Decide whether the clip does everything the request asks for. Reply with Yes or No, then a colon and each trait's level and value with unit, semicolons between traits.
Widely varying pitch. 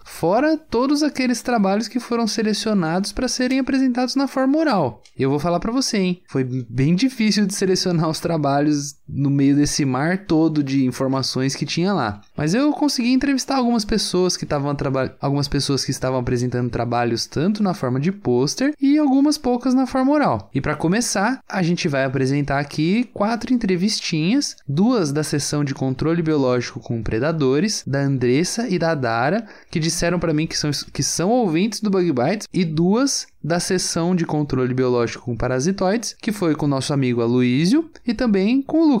Yes: wide, 8.9 semitones